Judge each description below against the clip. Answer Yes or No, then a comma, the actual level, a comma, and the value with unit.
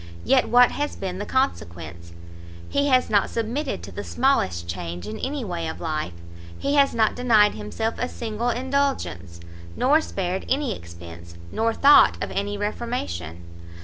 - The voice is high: Yes, high, 210 Hz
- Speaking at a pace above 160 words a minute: No, average, 155 wpm